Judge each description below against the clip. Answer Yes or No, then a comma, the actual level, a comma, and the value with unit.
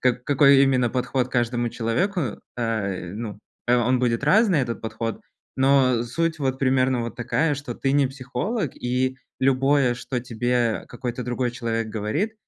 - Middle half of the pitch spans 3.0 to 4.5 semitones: No, narrow, 2.5 semitones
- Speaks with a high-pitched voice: No, low, 125 Hz